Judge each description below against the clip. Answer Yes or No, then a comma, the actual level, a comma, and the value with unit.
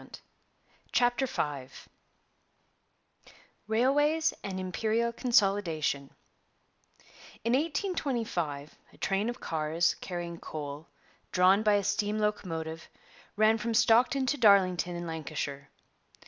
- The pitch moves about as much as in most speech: No, wide, 6.3 semitones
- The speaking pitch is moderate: No, high, 200 Hz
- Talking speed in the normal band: No, slow, 100 wpm